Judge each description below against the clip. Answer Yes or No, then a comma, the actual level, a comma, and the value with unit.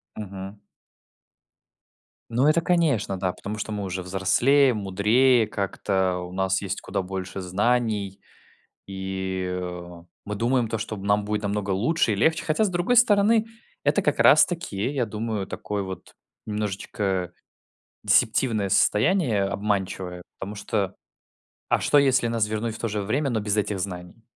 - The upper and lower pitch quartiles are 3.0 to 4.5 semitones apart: Yes, average, 3.7 semitones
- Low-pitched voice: Yes, low, 105 Hz